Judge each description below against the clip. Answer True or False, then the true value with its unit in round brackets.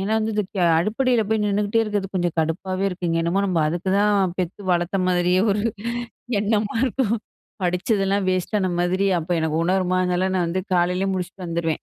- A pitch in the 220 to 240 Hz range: False (185 Hz)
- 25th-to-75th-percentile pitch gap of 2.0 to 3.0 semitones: True (2.6 semitones)